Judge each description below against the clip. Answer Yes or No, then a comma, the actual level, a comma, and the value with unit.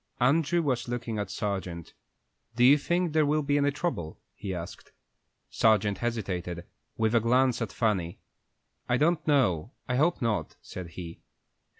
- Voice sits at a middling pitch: No, low, 120 Hz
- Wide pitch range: Yes, wide, 6.9 semitones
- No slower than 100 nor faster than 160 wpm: Yes, average, 155 wpm